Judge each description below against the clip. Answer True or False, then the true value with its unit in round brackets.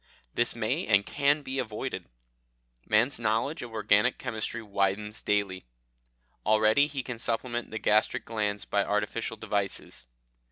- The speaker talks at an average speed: False (130 wpm)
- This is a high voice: False (110 Hz)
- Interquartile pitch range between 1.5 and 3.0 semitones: True (2.4 semitones)